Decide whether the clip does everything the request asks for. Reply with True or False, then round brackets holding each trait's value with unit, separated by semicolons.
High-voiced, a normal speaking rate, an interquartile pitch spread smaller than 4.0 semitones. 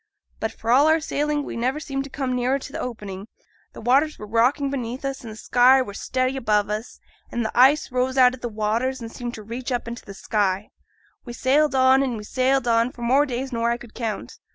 False (250 Hz; 235 wpm; 2.8 semitones)